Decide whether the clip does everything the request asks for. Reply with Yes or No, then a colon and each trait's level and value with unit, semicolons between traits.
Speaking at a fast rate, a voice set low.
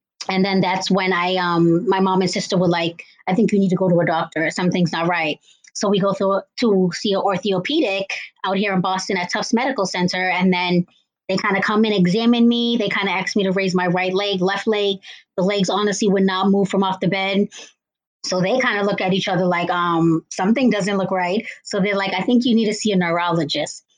No: fast, 240 wpm; high, 195 Hz